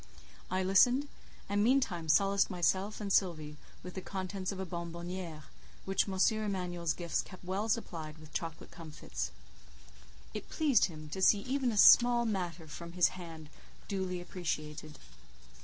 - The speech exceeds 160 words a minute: No, average, 145 wpm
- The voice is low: No, medium, 185 Hz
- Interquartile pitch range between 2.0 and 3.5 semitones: Yes, average, 3.2 semitones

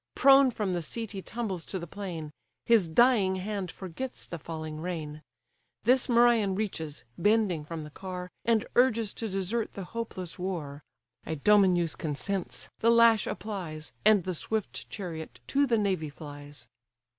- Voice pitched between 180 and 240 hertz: Yes, high, 190 Hz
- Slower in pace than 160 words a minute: Yes, average, 150 wpm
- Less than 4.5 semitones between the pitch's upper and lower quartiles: No, wide, 5.4 semitones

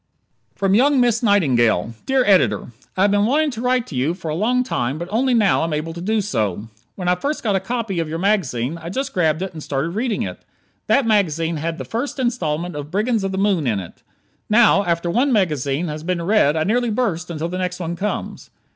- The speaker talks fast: Yes, fast, 230 wpm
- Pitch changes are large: Yes, wide, 5.8 semitones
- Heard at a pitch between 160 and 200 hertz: Yes, medium, 185 Hz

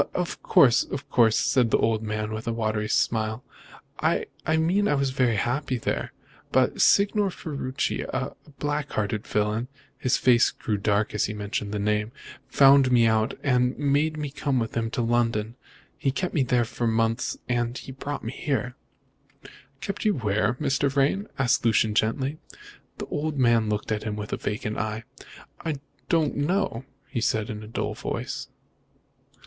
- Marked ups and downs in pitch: No, average, 4.2 semitones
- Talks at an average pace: Yes, average, 175 wpm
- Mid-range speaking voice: No, low, 120 Hz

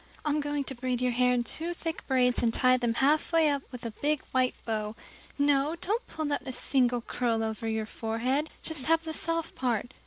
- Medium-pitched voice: No, very high, 260 Hz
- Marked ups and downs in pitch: No, average, 4.0 semitones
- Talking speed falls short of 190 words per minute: No, fast, 205 wpm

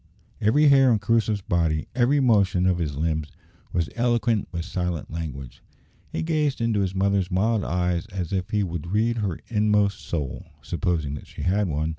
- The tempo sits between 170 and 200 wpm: Yes, average, 175 wpm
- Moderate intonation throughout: Yes, average, 4.8 semitones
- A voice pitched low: Yes, very low, 95 Hz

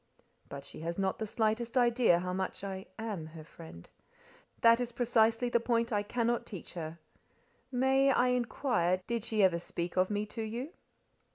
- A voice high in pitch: Yes, high, 220 Hz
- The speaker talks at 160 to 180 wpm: Yes, average, 175 wpm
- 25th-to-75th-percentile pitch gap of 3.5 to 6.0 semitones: Yes, average, 4.6 semitones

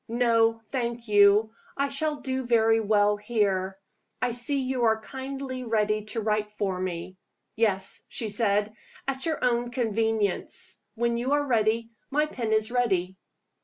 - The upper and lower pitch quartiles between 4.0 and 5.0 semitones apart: No, average, 3.0 semitones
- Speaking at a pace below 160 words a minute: Yes, average, 150 wpm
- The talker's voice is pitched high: Yes, high, 225 Hz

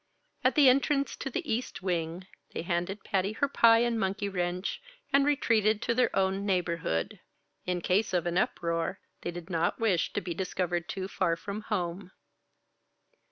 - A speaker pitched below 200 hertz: Yes, high, 190 Hz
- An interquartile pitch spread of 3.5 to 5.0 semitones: Yes, average, 4.2 semitones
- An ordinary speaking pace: Yes, average, 165 wpm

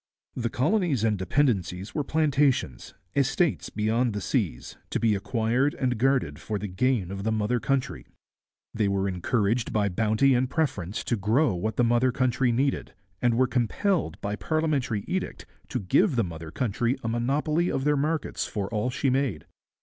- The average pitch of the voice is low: Yes, low, 120 Hz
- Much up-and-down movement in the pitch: No, average, 4.8 semitones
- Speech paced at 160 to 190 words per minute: Yes, average, 170 wpm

